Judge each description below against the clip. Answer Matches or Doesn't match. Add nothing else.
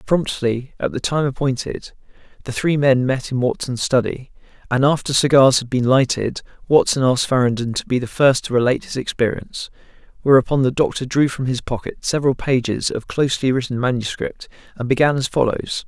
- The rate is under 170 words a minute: Doesn't match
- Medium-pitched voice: Doesn't match